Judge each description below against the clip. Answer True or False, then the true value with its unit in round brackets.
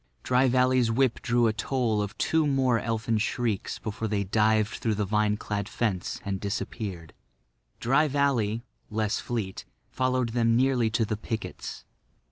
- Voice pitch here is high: False (115 Hz)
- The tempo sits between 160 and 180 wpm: False (150 wpm)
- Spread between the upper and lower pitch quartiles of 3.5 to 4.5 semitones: False (3.0 semitones)